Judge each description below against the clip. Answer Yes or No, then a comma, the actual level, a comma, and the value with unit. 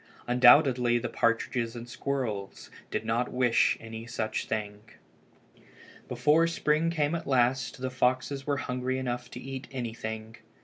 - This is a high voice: No, low, 125 Hz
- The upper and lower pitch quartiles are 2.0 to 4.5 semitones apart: Yes, narrow, 2.5 semitones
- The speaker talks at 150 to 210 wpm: No, average, 140 wpm